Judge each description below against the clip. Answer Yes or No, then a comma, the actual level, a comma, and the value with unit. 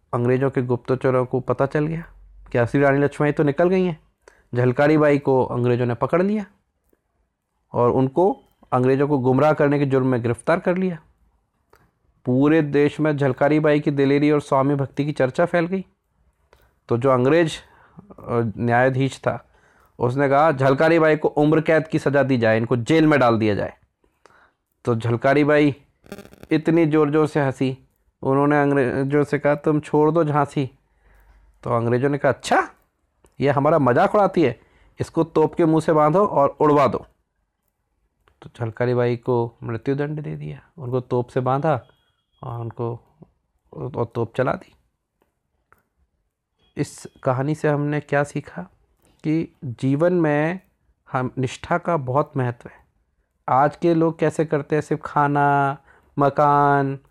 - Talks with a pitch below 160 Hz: Yes, medium, 140 Hz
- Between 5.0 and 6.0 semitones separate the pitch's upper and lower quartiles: No, average, 3.2 semitones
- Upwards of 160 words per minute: No, average, 155 wpm